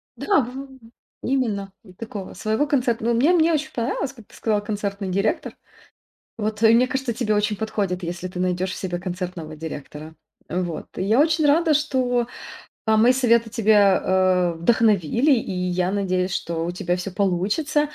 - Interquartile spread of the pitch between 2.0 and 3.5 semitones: No, average, 5.2 semitones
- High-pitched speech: Yes, high, 210 Hz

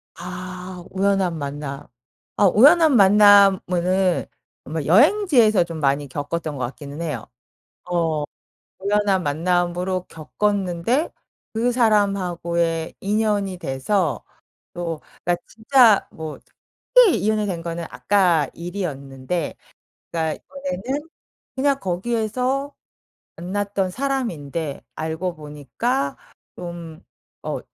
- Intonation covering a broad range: No, average, 4.5 semitones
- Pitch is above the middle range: No, medium, 180 Hz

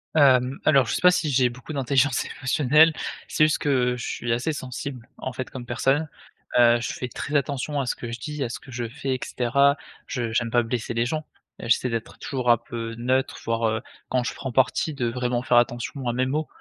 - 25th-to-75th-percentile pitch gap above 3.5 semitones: No, narrow, 2.6 semitones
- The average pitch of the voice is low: Yes, low, 125 Hz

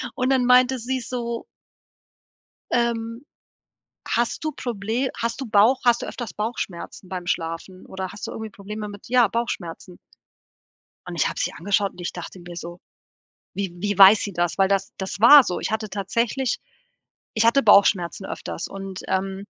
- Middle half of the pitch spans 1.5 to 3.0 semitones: No, average, 3.8 semitones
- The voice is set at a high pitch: Yes, high, 205 Hz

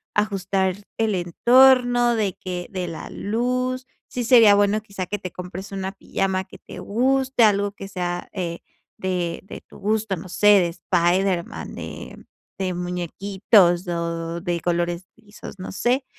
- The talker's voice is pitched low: No, high, 195 Hz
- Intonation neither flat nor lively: Yes, average, 3.6 semitones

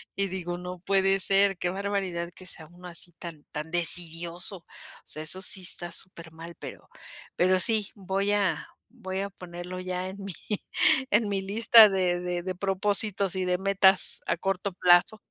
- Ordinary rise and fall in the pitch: No, narrow, 1.9 semitones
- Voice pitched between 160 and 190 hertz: Yes, medium, 185 Hz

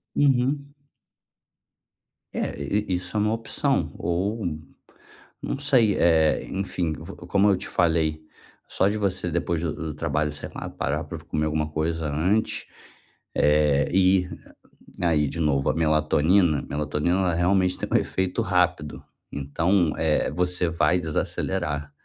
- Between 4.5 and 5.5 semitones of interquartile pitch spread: No, average, 3.7 semitones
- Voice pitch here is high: No, very low, 85 Hz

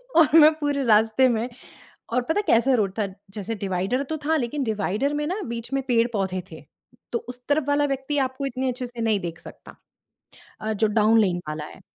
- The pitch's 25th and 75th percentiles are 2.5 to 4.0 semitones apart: No, average, 4.5 semitones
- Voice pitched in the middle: No, high, 235 Hz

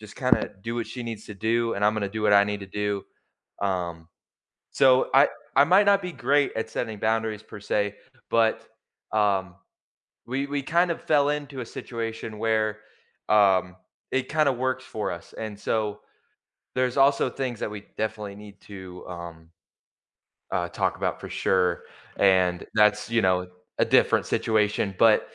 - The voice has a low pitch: Yes, low, 110 Hz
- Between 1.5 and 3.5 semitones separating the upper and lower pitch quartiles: No, average, 4.1 semitones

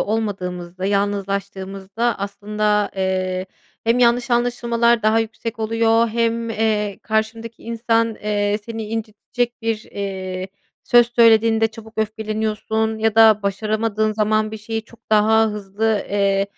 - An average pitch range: No, narrow, 1.9 semitones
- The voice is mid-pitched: No, high, 220 Hz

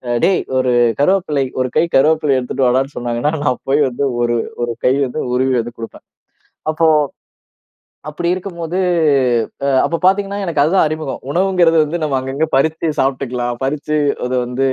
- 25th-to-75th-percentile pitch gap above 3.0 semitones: Yes, average, 4.3 semitones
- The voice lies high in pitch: No, medium, 145 Hz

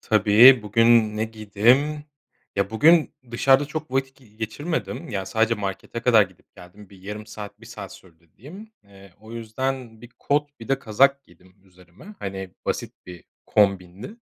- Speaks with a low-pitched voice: Yes, low, 110 Hz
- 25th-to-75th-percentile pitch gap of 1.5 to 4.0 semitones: No, average, 5.2 semitones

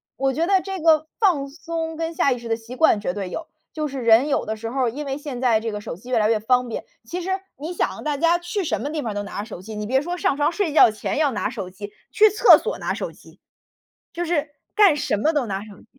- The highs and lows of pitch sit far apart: Yes, wide, 6.5 semitones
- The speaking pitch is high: Yes, very high, 275 Hz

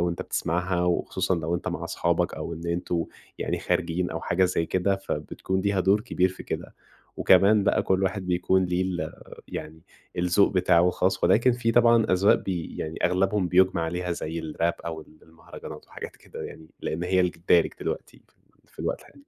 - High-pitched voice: No, very low, 90 Hz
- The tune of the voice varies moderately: No, narrow, 2.0 semitones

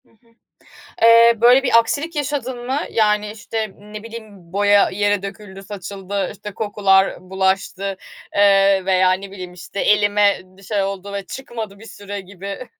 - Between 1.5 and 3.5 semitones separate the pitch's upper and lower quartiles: Yes, narrow, 2.4 semitones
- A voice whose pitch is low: No, high, 205 Hz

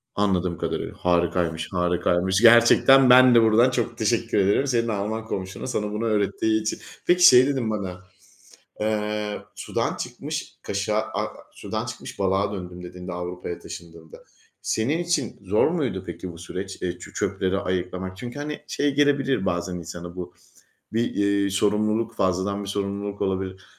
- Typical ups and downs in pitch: Yes, average, 4.0 semitones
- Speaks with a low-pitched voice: Yes, low, 100 Hz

